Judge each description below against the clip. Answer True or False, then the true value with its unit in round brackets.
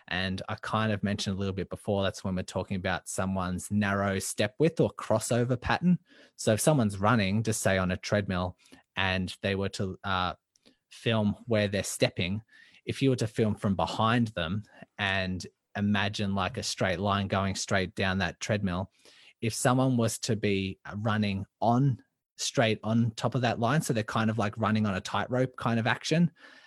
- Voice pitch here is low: True (105 Hz)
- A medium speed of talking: True (185 wpm)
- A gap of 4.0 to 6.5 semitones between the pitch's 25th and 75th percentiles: False (3.2 semitones)